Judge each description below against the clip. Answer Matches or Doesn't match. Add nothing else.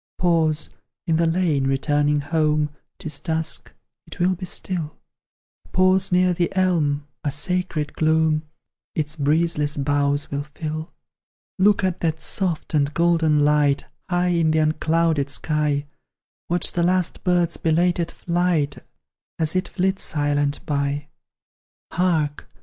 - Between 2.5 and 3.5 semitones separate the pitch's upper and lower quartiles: Matches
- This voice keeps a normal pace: Doesn't match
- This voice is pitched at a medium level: Matches